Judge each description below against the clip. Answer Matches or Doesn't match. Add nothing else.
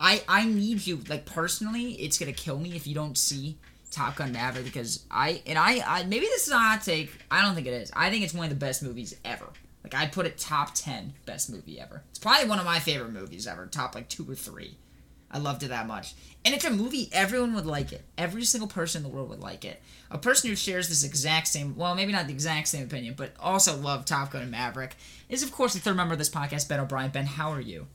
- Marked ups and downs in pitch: Matches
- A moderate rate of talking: Doesn't match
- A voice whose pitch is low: Doesn't match